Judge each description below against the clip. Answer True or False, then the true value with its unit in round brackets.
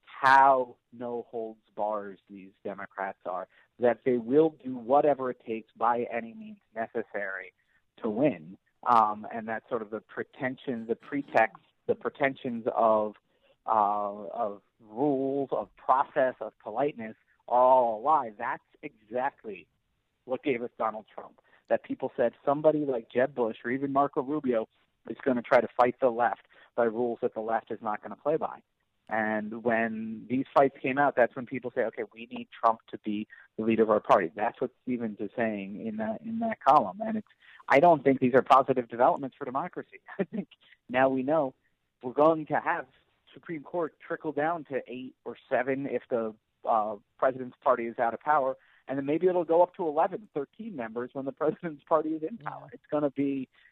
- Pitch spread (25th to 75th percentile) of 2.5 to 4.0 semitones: False (4.7 semitones)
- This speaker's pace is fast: False (190 wpm)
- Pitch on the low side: True (130 Hz)